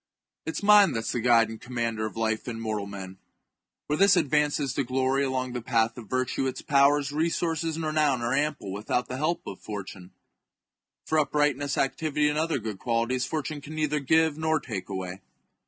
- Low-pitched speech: Yes, low, 130 Hz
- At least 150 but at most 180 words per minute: No, average, 190 wpm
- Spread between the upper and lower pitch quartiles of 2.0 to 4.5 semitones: No, average, 5.1 semitones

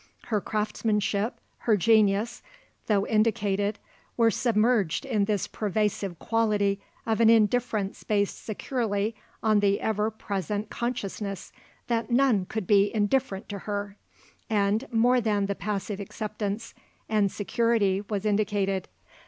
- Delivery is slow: Yes, slow, 120 wpm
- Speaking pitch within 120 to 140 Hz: No, high, 210 Hz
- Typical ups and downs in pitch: No, narrow, 2.0 semitones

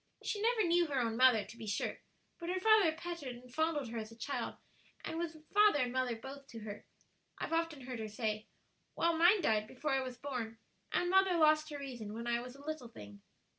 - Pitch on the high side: Yes, very high, 270 Hz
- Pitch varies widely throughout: Yes, wide, 6.1 semitones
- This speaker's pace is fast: Yes, fast, 220 wpm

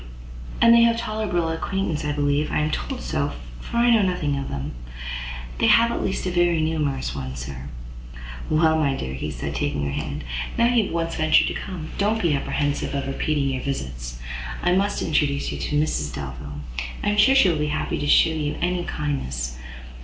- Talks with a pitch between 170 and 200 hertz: No, medium, 150 Hz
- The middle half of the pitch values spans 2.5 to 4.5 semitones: No, average, 5.2 semitones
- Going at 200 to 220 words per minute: Yes, fast, 205 wpm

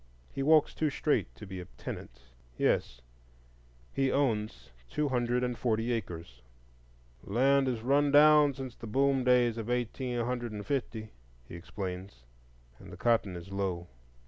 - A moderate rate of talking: Yes, average, 145 wpm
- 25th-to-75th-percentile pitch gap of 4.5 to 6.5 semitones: Yes, wide, 5.6 semitones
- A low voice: Yes, low, 120 Hz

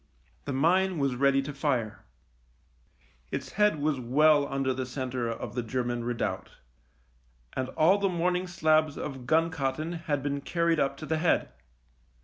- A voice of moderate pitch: Yes, medium, 145 Hz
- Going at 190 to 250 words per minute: No, average, 155 wpm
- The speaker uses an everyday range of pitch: Yes, average, 3.9 semitones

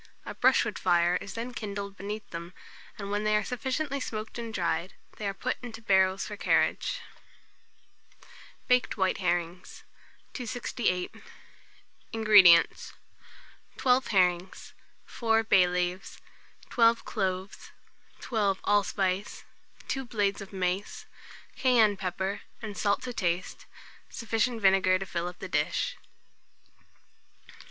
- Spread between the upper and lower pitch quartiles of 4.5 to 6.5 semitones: No, average, 3.6 semitones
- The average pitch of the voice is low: No, high, 200 Hz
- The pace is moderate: No, slow, 120 wpm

